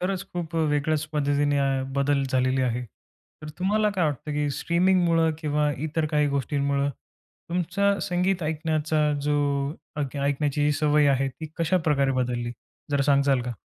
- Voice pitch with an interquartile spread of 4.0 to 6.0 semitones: No, average, 2.8 semitones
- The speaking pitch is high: No, medium, 150 Hz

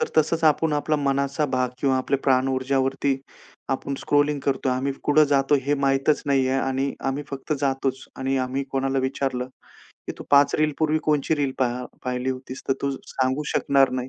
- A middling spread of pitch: No, narrow, 1.5 semitones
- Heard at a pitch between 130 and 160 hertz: Yes, low, 135 Hz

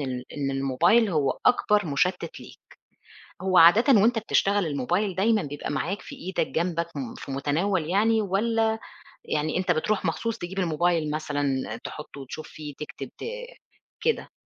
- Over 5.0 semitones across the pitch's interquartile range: Yes, wide, 5.4 semitones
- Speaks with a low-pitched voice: No, medium, 175 Hz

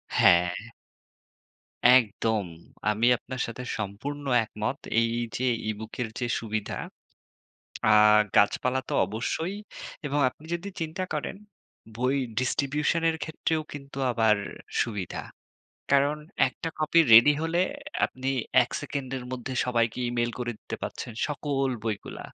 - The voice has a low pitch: Yes, low, 125 Hz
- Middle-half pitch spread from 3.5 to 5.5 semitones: Yes, average, 4.7 semitones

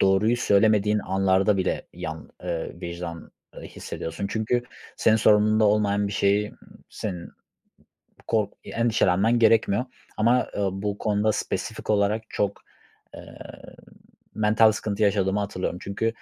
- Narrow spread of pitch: Yes, narrow, 2.0 semitones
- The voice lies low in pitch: Yes, low, 105 Hz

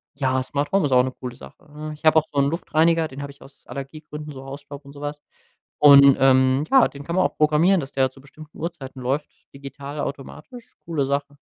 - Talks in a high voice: No, medium, 145 Hz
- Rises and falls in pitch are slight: Yes, narrow, 2.1 semitones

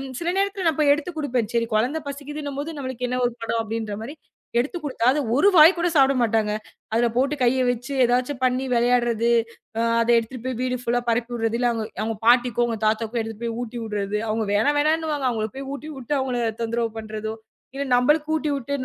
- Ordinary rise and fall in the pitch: Yes, average, 3.9 semitones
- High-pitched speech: Yes, high, 245 Hz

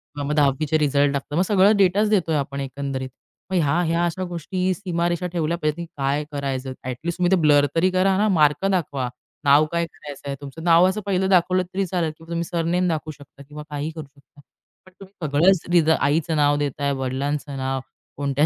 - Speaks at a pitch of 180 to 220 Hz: No, medium, 155 Hz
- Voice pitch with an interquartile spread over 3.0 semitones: Yes, average, 3.8 semitones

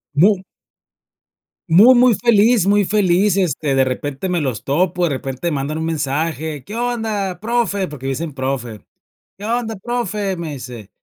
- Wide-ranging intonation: Yes, wide, 6.9 semitones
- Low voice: No, medium, 175 Hz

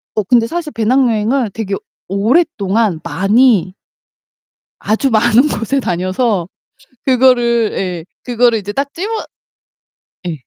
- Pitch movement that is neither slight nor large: Yes, average, 4.3 semitones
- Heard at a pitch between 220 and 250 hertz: Yes, high, 230 Hz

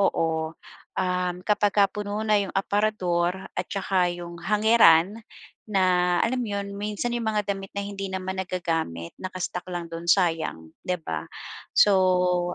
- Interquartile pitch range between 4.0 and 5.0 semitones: No, narrow, 2.6 semitones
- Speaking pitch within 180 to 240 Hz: Yes, medium, 185 Hz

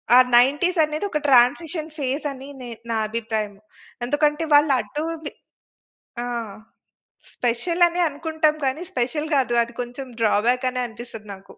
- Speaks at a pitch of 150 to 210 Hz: No, very high, 270 Hz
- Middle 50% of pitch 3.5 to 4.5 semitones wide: Yes, average, 4.2 semitones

